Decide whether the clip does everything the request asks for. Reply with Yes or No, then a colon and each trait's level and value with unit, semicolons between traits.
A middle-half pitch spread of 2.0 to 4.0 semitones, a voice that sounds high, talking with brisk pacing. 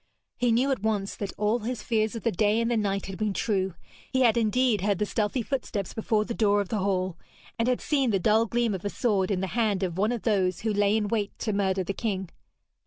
Yes: average, 2.8 semitones; high, 210 Hz; fast, 250 wpm